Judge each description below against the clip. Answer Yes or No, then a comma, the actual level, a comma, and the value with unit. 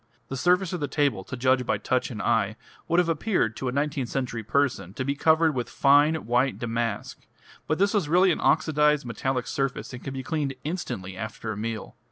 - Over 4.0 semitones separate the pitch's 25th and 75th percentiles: Yes, average, 4.8 semitones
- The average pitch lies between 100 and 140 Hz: Yes, low, 135 Hz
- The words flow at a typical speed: No, fast, 210 wpm